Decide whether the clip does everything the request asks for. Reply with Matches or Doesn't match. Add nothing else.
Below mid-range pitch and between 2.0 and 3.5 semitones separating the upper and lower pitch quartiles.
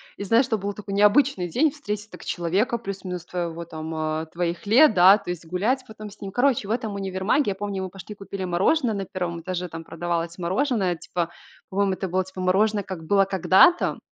Doesn't match